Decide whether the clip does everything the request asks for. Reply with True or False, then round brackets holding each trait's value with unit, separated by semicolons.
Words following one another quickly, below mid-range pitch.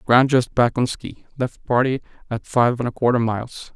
True (210 wpm; 120 Hz)